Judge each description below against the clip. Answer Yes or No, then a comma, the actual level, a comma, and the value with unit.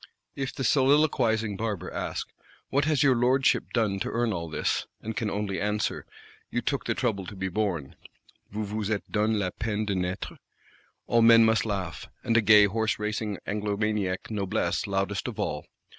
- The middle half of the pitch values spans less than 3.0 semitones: Yes, narrow, 2.5 semitones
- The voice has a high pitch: No, low, 105 Hz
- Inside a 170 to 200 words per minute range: Yes, average, 175 wpm